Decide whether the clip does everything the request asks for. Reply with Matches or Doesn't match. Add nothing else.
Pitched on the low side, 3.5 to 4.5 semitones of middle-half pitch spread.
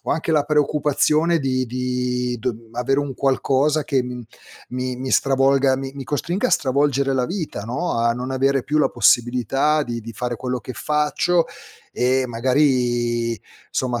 Doesn't match